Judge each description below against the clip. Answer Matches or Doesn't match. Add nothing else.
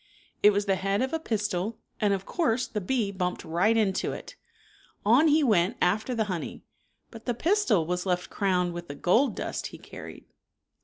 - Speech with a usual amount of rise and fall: Matches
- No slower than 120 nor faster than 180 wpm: Doesn't match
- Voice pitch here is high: Matches